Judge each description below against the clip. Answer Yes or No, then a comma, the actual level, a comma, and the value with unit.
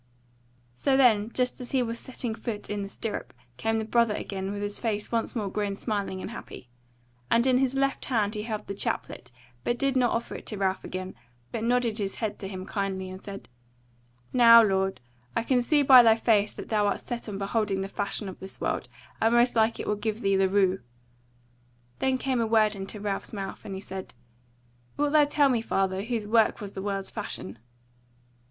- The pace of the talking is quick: Yes, fast, 210 wpm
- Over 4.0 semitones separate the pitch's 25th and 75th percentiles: No, average, 3.2 semitones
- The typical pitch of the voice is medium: No, high, 215 Hz